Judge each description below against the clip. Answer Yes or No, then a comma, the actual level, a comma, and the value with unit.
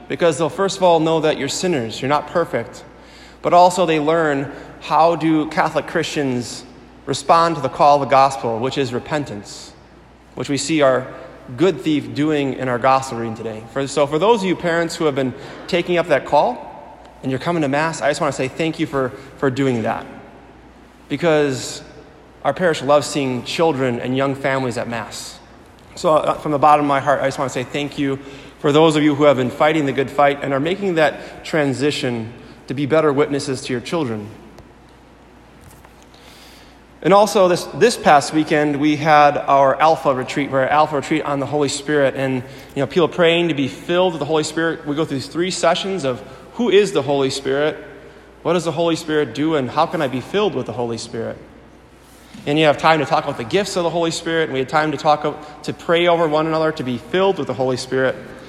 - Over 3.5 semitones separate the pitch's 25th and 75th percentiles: No, average, 3.2 semitones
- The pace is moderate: No, fast, 215 wpm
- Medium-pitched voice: Yes, medium, 145 Hz